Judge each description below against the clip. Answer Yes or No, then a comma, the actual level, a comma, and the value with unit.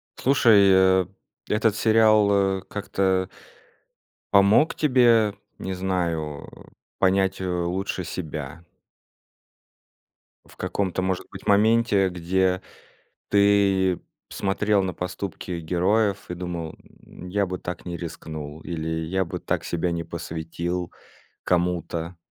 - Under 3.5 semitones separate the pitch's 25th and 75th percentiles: Yes, average, 2.7 semitones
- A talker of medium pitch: No, very low, 95 Hz